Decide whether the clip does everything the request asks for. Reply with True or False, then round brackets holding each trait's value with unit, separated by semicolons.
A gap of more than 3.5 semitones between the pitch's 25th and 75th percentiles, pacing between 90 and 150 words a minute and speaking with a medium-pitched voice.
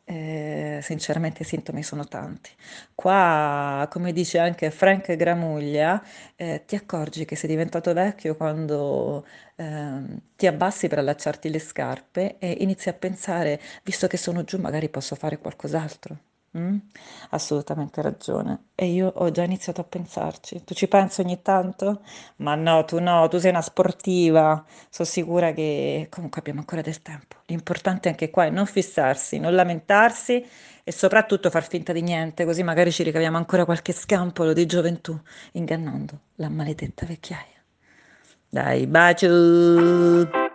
False (2.6 semitones; 145 wpm; 170 Hz)